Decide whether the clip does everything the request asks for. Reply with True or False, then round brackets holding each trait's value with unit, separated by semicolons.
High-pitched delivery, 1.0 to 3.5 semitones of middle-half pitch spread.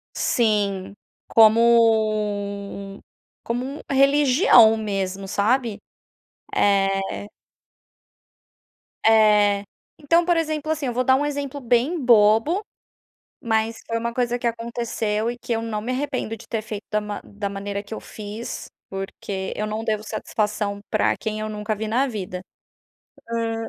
True (220 Hz; 2.8 semitones)